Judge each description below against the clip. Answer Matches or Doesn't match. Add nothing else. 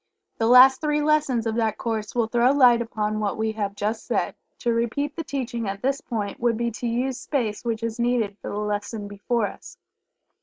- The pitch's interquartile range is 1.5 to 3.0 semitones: Matches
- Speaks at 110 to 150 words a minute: Doesn't match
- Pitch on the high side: Matches